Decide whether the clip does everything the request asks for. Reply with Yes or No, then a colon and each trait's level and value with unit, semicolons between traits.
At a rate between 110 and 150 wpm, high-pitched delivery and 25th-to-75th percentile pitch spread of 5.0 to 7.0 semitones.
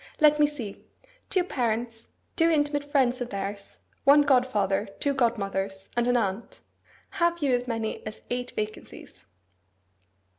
Yes: average, 140 wpm; high, 245 Hz; average, 5.3 semitones